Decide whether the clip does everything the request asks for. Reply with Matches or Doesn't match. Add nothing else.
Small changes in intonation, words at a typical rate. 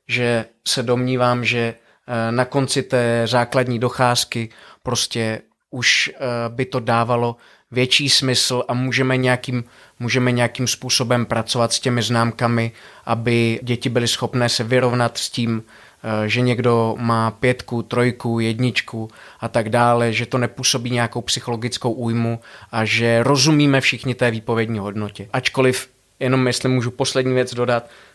Matches